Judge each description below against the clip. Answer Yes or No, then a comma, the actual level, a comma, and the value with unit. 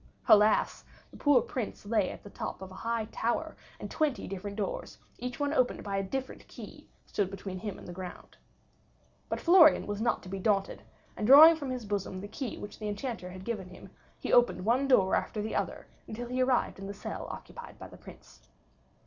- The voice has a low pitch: No, high, 215 Hz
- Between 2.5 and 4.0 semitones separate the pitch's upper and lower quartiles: No, average, 4.4 semitones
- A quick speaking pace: Yes, fast, 210 wpm